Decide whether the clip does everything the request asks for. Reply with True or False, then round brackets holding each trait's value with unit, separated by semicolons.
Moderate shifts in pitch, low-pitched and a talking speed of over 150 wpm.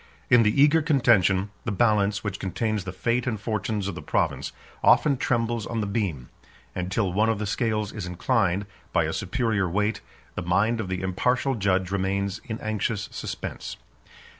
True (3.3 semitones; 105 Hz; 175 wpm)